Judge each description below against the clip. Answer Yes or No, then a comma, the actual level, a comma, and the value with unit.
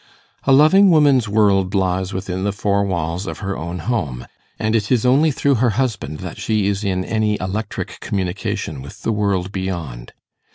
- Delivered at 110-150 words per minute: No, average, 175 wpm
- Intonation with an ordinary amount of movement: Yes, average, 3.4 semitones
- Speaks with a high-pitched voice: No, low, 100 Hz